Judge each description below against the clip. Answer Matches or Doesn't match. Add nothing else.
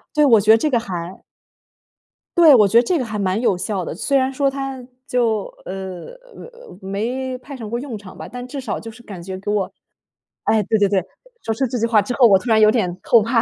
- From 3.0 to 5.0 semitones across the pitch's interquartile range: Matches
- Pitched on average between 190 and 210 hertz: Doesn't match